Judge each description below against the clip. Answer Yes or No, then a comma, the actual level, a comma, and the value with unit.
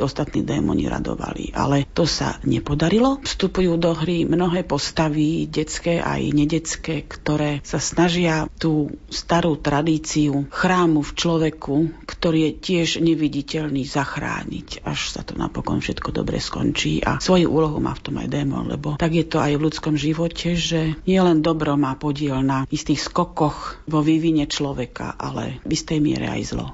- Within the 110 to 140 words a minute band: No, average, 155 wpm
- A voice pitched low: No, medium, 155 Hz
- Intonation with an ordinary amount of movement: No, narrow, 2.1 semitones